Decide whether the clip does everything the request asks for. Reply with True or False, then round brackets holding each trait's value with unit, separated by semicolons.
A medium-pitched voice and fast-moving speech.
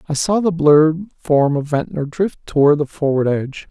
False (155 Hz; 195 wpm)